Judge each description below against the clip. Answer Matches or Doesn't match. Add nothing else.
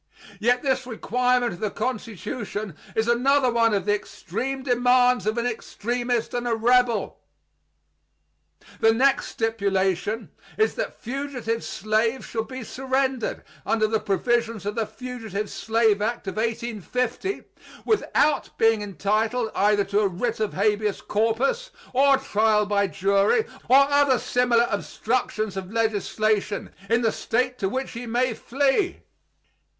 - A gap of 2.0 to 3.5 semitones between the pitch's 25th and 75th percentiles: Matches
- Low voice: Doesn't match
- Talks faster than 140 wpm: Doesn't match